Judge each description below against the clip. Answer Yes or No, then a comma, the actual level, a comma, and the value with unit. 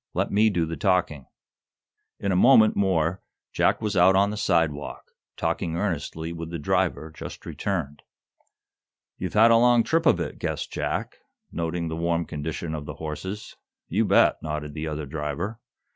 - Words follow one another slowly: No, average, 165 wpm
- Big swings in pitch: No, average, 4.2 semitones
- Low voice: Yes, very low, 85 Hz